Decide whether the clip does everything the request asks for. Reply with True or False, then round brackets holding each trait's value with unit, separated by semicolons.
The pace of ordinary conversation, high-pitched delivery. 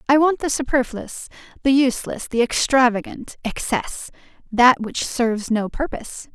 False (130 wpm; 250 Hz)